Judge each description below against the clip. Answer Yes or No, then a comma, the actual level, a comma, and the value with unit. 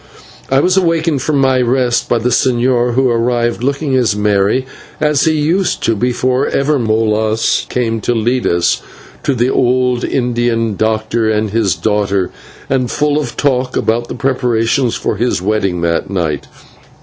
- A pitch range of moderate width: Yes, average, 3.2 semitones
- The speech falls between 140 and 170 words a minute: Yes, average, 160 wpm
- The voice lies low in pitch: Yes, low, 120 Hz